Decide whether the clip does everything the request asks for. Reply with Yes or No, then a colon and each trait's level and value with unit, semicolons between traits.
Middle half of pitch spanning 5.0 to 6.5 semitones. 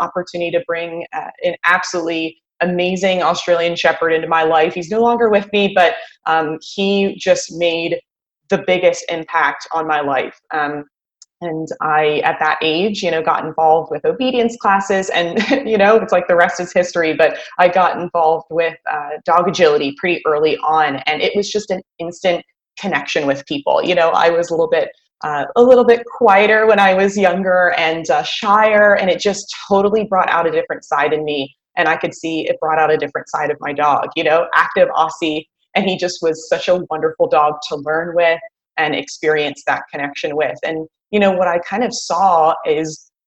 No: average, 3.7 semitones